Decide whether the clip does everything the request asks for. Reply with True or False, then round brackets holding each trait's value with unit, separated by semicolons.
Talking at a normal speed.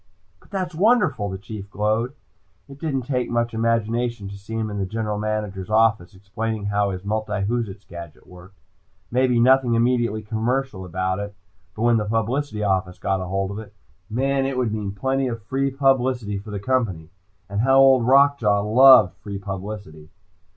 True (170 wpm)